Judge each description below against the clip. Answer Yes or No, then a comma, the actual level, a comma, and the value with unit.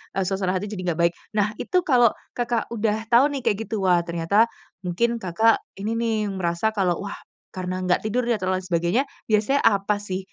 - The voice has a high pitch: Yes, high, 205 Hz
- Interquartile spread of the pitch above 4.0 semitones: No, average, 3.7 semitones